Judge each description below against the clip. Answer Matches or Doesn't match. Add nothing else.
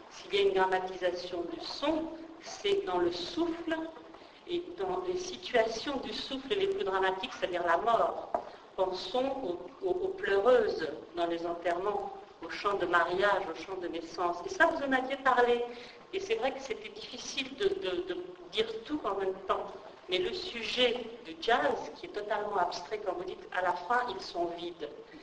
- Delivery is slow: Doesn't match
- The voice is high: Matches